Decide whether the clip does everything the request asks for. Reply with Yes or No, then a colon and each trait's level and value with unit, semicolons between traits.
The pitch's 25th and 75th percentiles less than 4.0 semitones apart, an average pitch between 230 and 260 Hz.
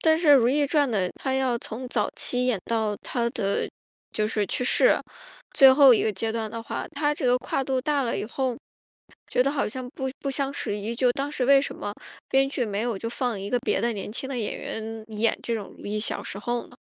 Yes: average, 3.5 semitones; high, 245 Hz